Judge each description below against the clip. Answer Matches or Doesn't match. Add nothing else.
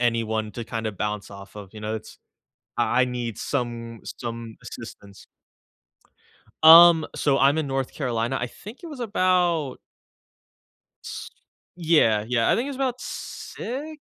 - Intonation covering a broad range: Matches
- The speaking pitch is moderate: Doesn't match